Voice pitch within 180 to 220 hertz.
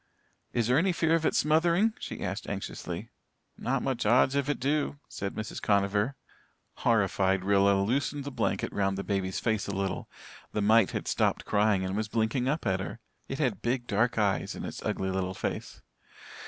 No: low, 110 Hz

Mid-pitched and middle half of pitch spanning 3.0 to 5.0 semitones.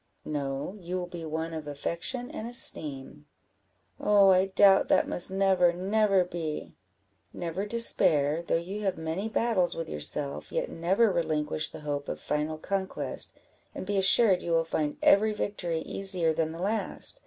Yes: medium, 175 Hz; average, 3.8 semitones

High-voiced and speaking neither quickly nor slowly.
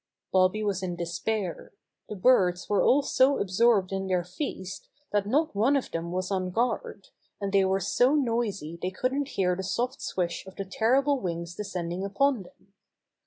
Yes: high, 195 Hz; average, 175 wpm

